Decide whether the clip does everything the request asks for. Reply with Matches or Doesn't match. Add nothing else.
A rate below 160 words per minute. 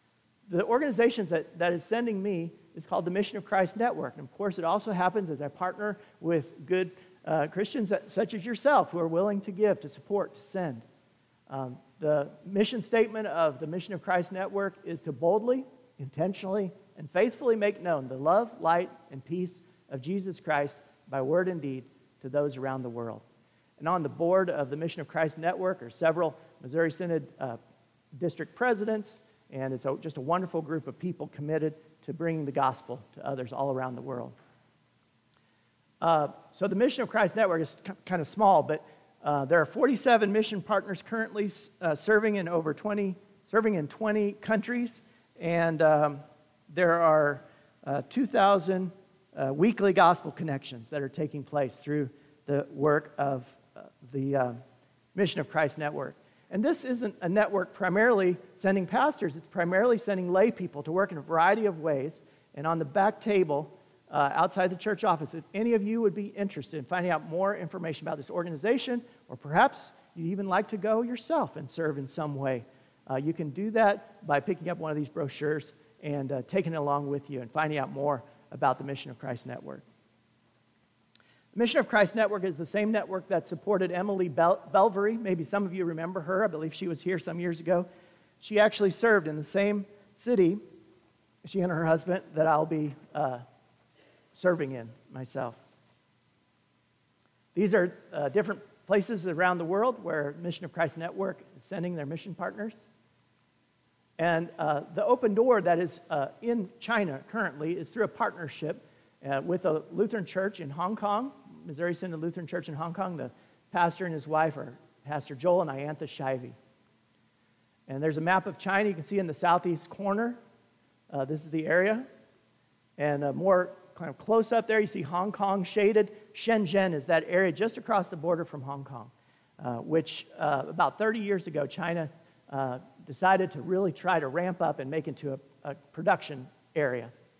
Doesn't match